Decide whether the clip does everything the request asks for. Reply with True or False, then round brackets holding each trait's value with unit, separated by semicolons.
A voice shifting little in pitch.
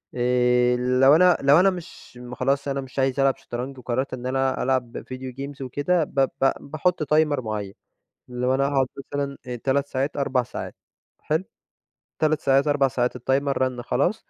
True (2.1 semitones)